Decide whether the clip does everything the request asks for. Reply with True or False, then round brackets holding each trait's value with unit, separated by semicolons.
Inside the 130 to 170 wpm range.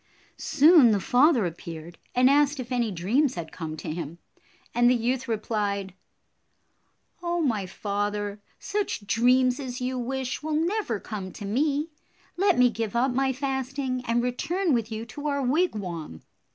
True (155 wpm)